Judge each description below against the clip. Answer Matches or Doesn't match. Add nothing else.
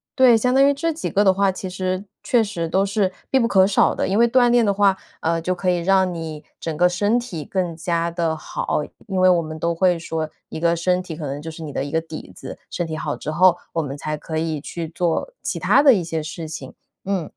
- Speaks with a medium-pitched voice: Matches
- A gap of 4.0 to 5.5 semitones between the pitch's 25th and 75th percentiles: Doesn't match